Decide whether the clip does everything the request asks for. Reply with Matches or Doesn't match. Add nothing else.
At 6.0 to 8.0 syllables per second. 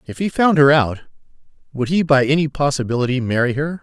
Matches